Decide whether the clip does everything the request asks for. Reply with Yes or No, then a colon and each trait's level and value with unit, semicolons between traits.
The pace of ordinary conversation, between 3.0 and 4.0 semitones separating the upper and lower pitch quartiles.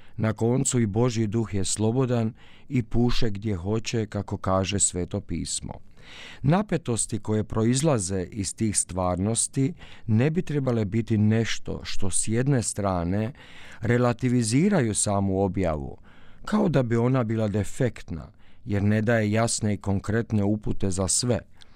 Yes: average, 130 wpm; average, 3.5 semitones